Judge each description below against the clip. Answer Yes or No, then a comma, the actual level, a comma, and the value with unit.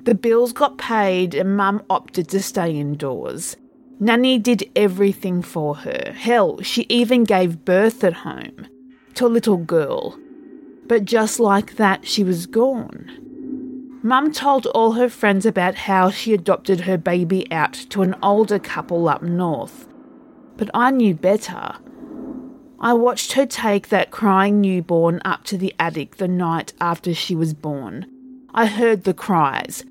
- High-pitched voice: Yes, high, 210 Hz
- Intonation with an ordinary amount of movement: No, wide, 5.8 semitones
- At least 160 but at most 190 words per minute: No, average, 150 wpm